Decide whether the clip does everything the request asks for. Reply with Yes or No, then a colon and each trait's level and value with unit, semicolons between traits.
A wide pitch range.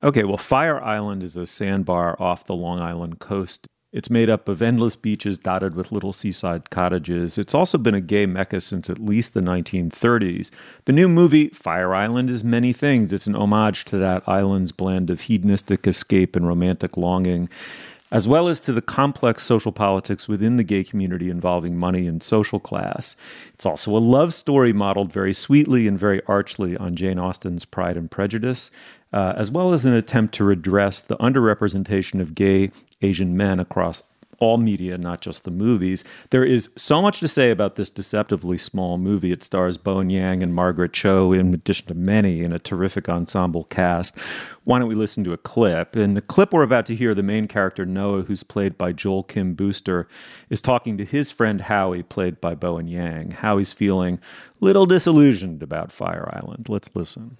No: average, 3.8 semitones